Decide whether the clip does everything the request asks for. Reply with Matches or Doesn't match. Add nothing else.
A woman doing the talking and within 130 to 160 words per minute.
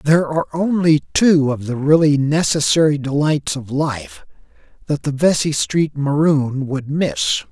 Doesn't match